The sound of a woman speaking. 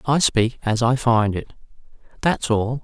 No: male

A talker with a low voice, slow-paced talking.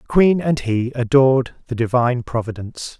No: low, 125 Hz; average, 160 wpm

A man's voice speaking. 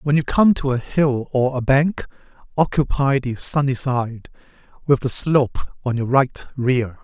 Yes: male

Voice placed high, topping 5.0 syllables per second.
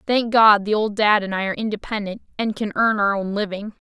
Yes: high, 210 Hz; 5.8 syllables/s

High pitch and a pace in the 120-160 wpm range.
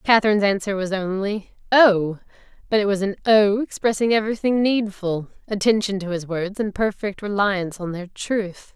Yes: high, 205 Hz; average, 150 wpm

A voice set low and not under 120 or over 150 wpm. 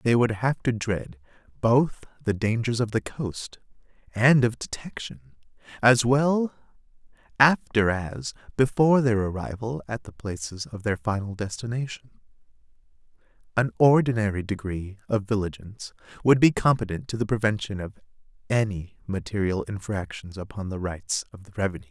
Yes: low, 110 Hz; slow, 135 wpm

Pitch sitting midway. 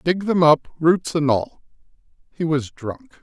Yes: medium, 155 Hz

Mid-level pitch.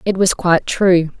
Yes: medium, 180 Hz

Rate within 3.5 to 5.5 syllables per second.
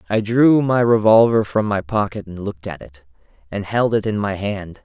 Yes: 5.0 syllables/s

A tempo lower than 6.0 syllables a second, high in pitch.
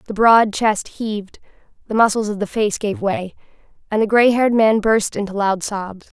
Yes: 4.9 syllables/s; high, 210 Hz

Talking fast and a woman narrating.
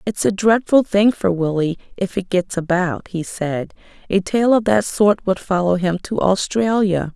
No: average, 185 wpm; female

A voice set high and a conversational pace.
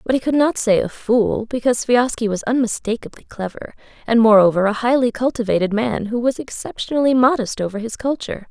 Yes: high, 230 Hz; average, 175 wpm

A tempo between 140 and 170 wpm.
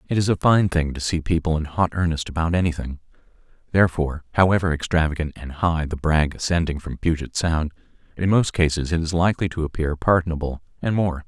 No: average, 185 wpm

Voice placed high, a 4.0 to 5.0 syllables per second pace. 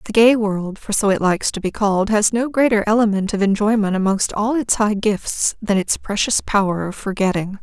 No: high, 205 Hz; 5.3 syllables/s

